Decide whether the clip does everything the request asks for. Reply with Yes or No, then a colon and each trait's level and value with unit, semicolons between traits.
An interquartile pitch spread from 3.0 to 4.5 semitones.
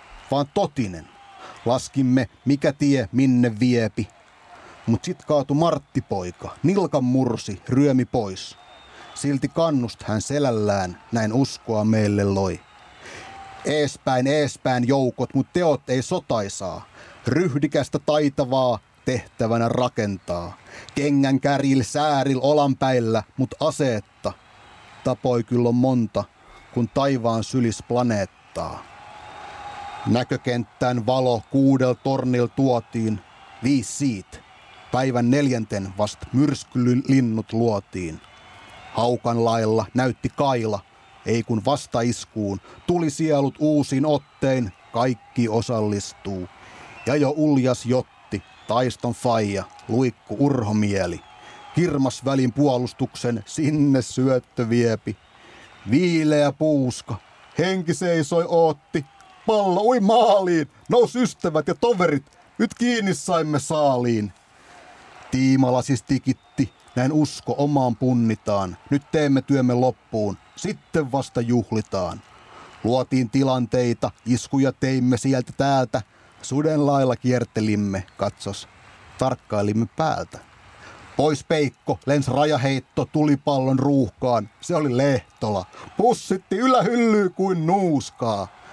Yes: average, 4.1 semitones